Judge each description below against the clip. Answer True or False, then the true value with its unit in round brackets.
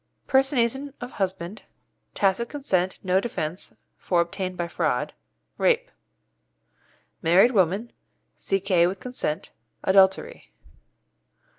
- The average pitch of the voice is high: True (195 Hz)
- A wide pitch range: False (4.9 semitones)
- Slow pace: True (95 wpm)